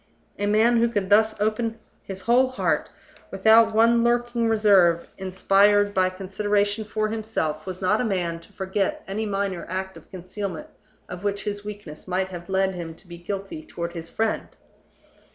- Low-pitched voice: No, high, 205 Hz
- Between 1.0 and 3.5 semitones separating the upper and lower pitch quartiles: Yes, average, 2.8 semitones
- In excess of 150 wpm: Yes, average, 170 wpm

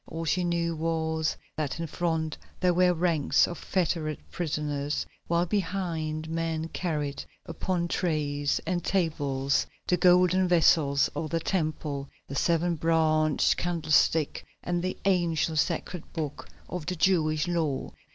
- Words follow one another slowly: Yes, slow, 130 wpm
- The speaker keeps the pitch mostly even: Yes, narrow, 2.3 semitones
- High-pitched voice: No, medium, 165 Hz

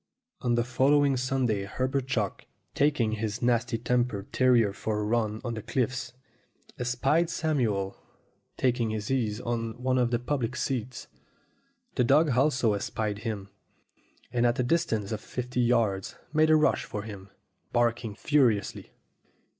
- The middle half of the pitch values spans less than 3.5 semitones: Yes, average, 3.0 semitones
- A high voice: No, low, 120 Hz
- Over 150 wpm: No, average, 145 wpm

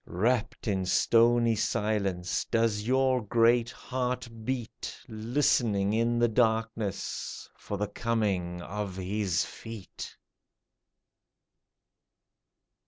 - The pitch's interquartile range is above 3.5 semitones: No, average, 2.8 semitones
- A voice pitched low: Yes, low, 110 Hz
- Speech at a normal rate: No, slow, 90 wpm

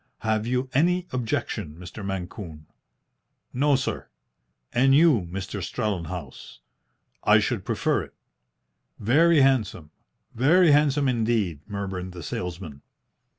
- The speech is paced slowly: Yes, slow, 110 wpm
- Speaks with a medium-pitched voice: No, low, 110 Hz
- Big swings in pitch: Yes, wide, 6.9 semitones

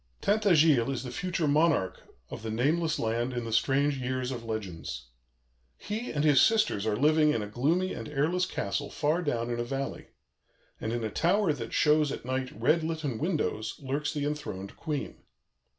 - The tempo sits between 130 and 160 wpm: No, average, 180 wpm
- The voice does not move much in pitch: No, average, 5.0 semitones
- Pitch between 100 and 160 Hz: Yes, medium, 140 Hz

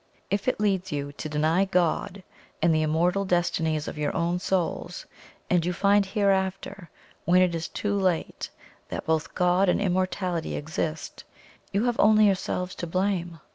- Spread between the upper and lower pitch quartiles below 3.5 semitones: Yes, average, 2.9 semitones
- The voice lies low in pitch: No, medium, 180 Hz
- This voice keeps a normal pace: Yes, average, 160 wpm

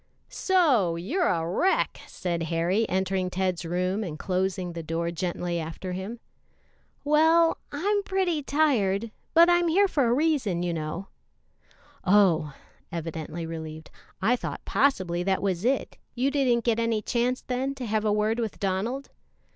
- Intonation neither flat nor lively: No, wide, 7.6 semitones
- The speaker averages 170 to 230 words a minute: No, average, 150 wpm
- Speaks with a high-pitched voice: Yes, high, 200 Hz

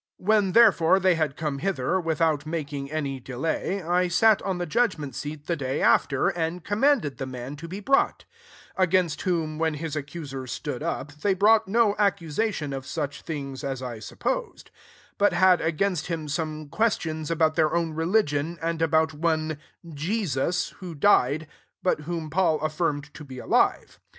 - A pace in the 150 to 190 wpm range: Yes, average, 175 wpm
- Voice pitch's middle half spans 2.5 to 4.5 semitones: Yes, average, 3.7 semitones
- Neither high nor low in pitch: Yes, medium, 160 Hz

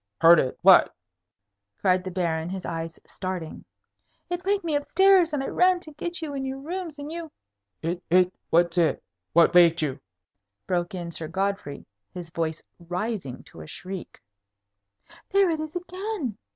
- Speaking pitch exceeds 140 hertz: Yes, medium, 185 Hz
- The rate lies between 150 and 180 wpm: Yes, average, 170 wpm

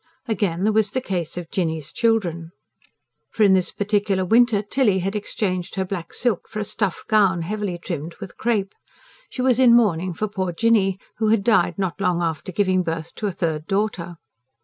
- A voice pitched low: No, high, 195 Hz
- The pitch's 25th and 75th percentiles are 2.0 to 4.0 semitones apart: Yes, average, 3.6 semitones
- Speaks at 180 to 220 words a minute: Yes, average, 190 wpm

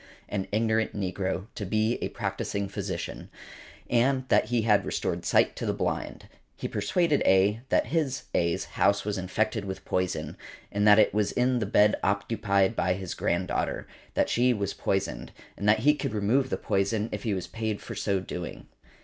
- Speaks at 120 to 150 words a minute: No, average, 180 wpm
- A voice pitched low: Yes, low, 105 Hz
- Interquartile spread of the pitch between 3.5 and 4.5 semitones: No, average, 2.8 semitones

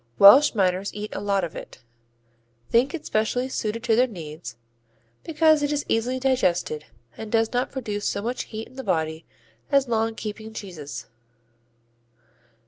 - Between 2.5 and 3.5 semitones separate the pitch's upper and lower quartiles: No, average, 4.8 semitones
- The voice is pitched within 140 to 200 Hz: No, high, 220 Hz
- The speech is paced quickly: No, average, 155 wpm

